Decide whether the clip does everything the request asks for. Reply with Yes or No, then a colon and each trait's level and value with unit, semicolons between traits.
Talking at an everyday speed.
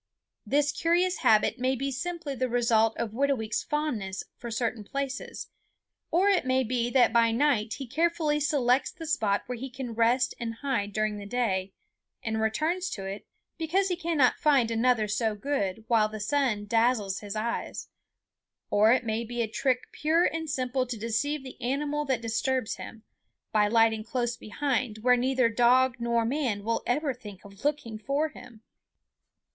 Yes: average, 170 wpm